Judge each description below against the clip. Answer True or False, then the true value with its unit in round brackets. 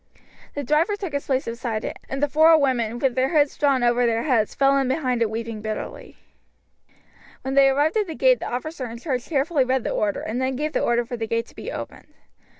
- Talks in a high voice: True (260 Hz)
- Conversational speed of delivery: False (235 wpm)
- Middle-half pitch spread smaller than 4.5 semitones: True (3.7 semitones)